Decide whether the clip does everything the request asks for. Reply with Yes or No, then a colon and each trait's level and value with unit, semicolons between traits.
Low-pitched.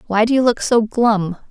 No: high, 220 Hz